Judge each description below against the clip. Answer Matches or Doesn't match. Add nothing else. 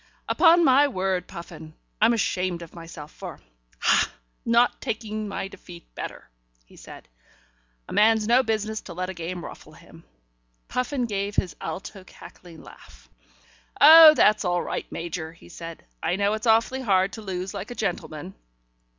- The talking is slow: Doesn't match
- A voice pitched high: Matches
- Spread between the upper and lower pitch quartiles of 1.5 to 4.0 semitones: Doesn't match